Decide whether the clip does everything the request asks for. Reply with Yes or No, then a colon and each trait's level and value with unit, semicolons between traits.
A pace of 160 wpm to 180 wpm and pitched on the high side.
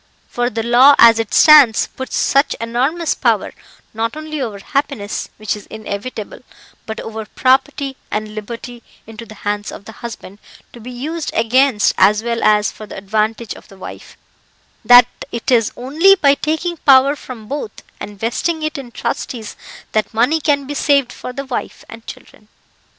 Yes: average, 170 wpm; high, 240 Hz